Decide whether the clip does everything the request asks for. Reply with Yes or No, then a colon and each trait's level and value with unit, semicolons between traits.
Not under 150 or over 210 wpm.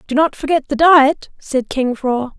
Yes: average, 200 wpm